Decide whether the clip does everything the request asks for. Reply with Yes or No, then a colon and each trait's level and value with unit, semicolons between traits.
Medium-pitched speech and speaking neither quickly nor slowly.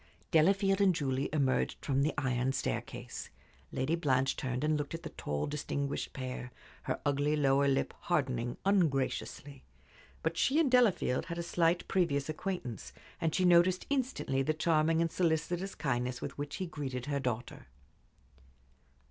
Yes: medium, 150 Hz; average, 150 wpm